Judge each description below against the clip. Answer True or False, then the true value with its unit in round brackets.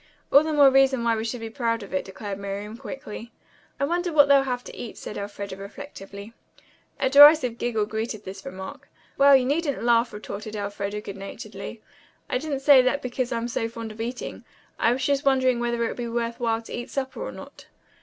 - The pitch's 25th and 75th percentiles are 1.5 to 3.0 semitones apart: False (4.2 semitones)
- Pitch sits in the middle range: False (235 Hz)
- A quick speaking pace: True (210 wpm)